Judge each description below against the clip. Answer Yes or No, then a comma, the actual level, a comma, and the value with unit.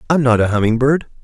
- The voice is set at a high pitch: No, low, 125 Hz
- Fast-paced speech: Yes, fast, 240 wpm